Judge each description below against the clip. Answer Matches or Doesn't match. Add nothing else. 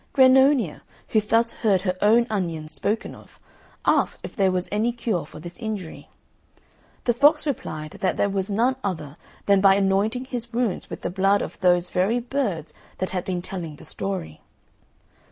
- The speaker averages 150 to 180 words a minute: Matches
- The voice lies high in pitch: Matches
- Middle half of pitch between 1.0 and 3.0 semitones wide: Doesn't match